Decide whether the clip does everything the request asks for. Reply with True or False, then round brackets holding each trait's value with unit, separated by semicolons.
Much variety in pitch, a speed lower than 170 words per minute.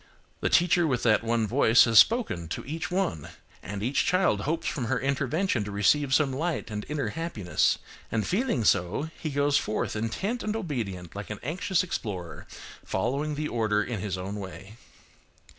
False (7.2 semitones; 175 wpm)